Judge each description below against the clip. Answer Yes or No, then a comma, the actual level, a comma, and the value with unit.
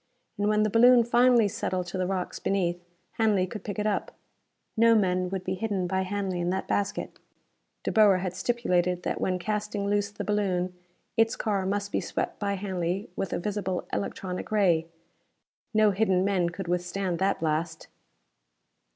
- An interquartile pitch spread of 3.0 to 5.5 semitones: No, narrow, 2.5 semitones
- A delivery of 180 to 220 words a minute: No, average, 170 wpm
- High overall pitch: Yes, high, 195 Hz